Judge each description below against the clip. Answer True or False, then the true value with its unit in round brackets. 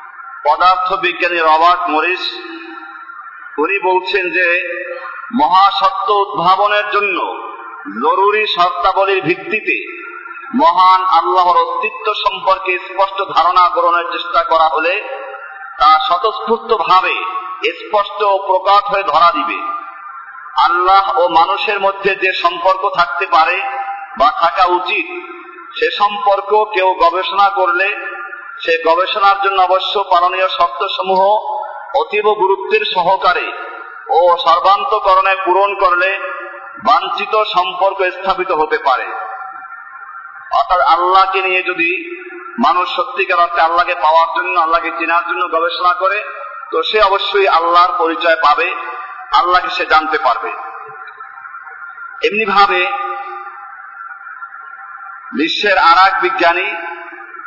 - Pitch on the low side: False (195 Hz)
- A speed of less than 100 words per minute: True (85 wpm)